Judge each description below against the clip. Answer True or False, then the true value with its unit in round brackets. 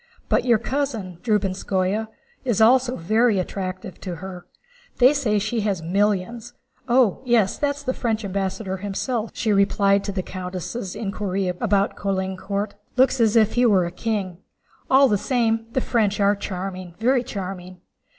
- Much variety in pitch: False (3.7 semitones)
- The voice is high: True (205 Hz)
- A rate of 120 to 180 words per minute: True (150 wpm)